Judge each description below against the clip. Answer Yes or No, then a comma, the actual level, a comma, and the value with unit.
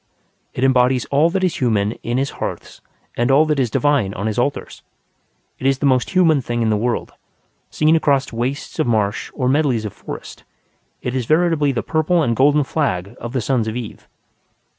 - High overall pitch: No, low, 130 Hz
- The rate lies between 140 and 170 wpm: No, average, 195 wpm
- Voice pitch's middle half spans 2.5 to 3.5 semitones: No, average, 3.9 semitones